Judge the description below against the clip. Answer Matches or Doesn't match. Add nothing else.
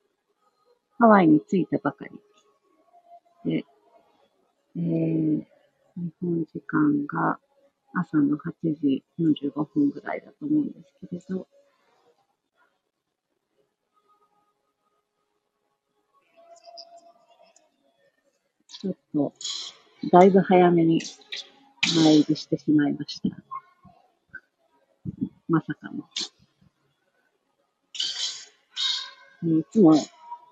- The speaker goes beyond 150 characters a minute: Doesn't match